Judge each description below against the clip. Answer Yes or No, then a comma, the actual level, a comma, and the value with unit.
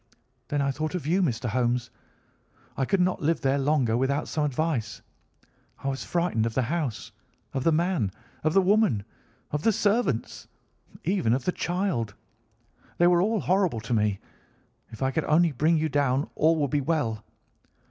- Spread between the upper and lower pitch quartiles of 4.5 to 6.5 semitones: Yes, wide, 5.6 semitones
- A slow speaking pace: No, average, 175 wpm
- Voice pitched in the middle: Yes, medium, 145 Hz